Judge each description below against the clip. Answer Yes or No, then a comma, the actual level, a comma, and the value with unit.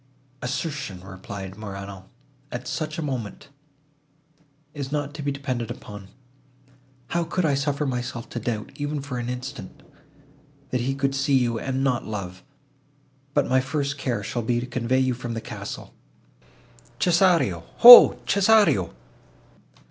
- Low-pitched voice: Yes, low, 130 Hz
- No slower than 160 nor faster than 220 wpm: No, slow, 135 wpm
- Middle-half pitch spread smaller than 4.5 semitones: Yes, average, 4.1 semitones